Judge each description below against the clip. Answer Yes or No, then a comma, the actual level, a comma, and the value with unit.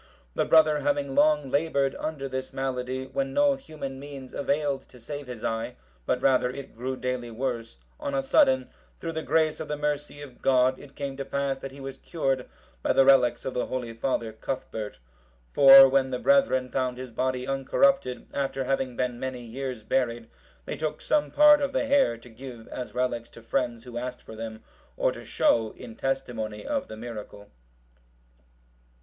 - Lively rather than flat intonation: No, narrow, 2.4 semitones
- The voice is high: No, low, 130 Hz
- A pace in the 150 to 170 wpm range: No, average, 185 wpm